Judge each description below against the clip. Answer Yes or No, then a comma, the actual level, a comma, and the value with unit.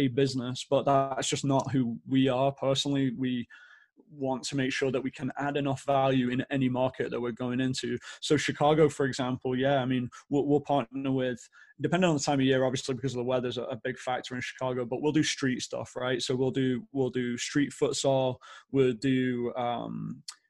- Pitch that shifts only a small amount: Yes, narrow, 1.5 semitones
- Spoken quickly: Yes, fast, 210 wpm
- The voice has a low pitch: Yes, low, 130 Hz